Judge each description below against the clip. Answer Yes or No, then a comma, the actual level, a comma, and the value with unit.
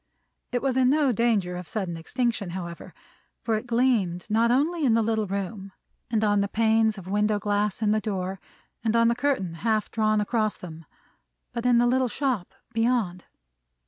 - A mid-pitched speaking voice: No, high, 220 Hz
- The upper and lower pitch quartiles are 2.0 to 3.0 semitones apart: No, average, 3.4 semitones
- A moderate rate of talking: Yes, average, 180 wpm